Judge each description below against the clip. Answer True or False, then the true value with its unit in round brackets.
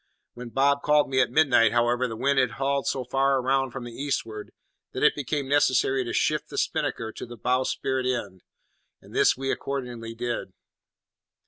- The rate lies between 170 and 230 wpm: True (180 wpm)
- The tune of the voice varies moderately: False (2.3 semitones)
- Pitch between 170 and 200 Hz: False (130 Hz)